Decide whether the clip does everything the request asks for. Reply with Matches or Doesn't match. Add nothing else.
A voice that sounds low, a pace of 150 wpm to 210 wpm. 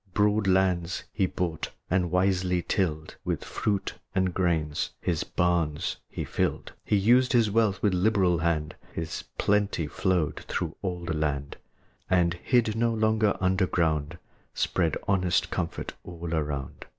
Doesn't match